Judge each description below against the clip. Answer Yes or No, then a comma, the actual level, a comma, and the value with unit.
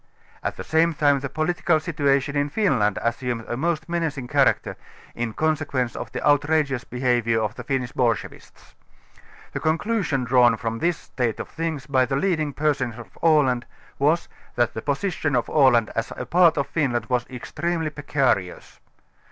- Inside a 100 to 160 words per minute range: No, average, 170 wpm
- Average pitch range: Yes, average, 4.4 semitones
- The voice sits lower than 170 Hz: Yes, medium, 140 Hz